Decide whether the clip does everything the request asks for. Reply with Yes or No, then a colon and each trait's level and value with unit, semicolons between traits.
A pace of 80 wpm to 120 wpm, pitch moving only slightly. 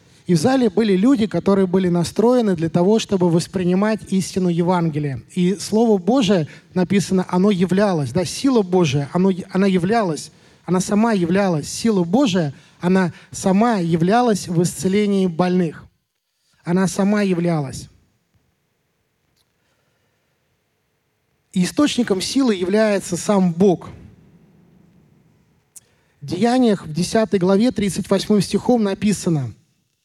No: slow, 110 wpm; average, 3.2 semitones